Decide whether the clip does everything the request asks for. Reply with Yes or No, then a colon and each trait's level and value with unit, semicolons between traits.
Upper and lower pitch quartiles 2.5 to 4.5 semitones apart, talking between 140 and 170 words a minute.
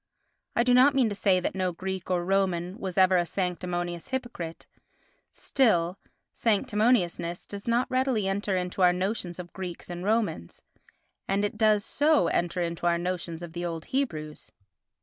Yes: average, 3.5 semitones; average, 165 wpm